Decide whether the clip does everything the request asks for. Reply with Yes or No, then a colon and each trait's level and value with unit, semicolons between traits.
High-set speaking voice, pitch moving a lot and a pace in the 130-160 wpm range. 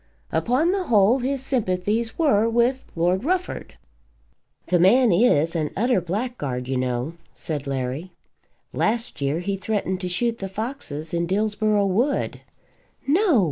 Yes: high, 205 Hz; wide, 6.3 semitones; average, 140 wpm